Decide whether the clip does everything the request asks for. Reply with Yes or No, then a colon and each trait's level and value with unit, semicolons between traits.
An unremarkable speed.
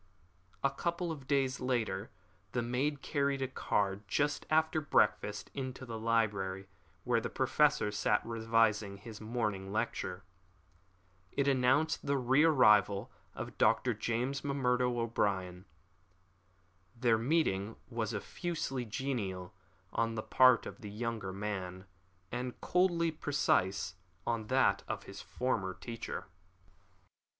No: slow, 120 wpm